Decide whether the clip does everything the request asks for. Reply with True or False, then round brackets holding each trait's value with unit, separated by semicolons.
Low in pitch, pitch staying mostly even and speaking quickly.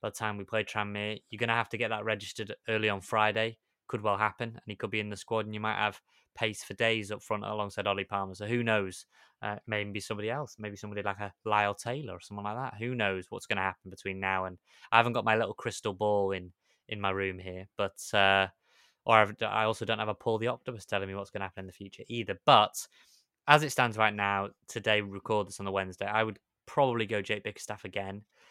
True (105 Hz; 2.0 semitones; 250 wpm)